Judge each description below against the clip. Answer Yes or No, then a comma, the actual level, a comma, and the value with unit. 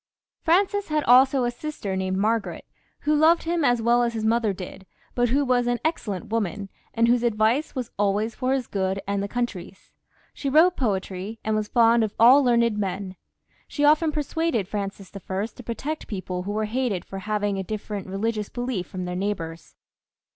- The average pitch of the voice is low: No, high, 225 Hz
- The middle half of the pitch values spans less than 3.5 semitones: No, average, 4.3 semitones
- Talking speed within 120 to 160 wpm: No, average, 185 wpm